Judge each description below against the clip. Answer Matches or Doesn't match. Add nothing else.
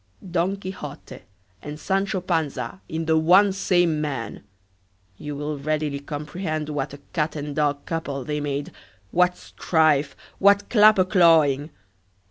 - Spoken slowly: Matches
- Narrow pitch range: Doesn't match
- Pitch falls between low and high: Matches